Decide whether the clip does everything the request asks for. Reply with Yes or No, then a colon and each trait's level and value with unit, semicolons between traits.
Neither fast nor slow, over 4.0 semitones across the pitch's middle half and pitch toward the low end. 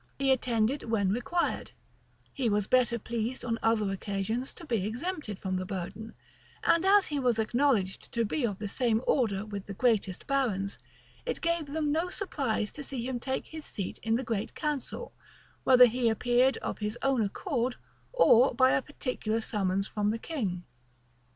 No: average, 175 wpm; average, 4.4 semitones; high, 235 Hz